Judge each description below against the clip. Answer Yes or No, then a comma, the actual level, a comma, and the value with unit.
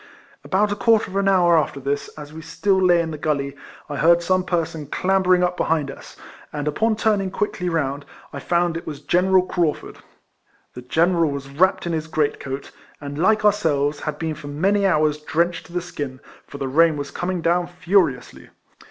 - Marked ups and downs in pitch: No, average, 4.0 semitones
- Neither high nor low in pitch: Yes, medium, 165 Hz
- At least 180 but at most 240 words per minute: Yes, average, 195 wpm